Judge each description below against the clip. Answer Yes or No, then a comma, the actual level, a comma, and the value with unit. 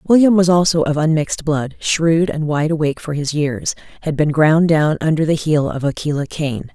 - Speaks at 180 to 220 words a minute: Yes, average, 195 wpm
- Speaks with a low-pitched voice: No, medium, 155 Hz